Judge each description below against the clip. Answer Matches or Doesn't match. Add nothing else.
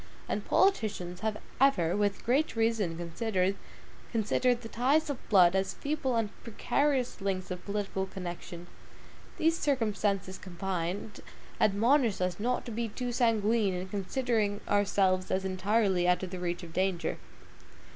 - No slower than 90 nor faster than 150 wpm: Matches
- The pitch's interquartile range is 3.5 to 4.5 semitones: Matches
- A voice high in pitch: Matches